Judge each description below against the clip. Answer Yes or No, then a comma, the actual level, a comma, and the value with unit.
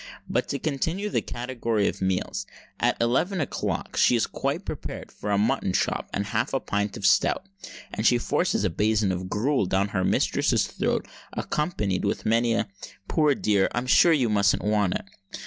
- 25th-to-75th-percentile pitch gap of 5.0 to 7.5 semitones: Yes, average, 5.3 semitones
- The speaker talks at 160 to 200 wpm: Yes, average, 175 wpm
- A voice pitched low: Yes, low, 110 Hz